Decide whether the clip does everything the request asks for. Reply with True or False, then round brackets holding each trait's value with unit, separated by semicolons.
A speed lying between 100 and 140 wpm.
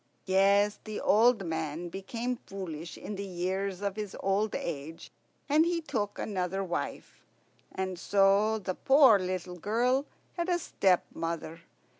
True (135 wpm)